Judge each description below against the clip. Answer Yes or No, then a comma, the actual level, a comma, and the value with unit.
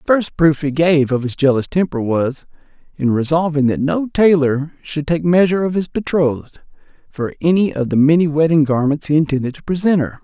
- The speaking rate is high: No, average, 195 wpm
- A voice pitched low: No, medium, 155 Hz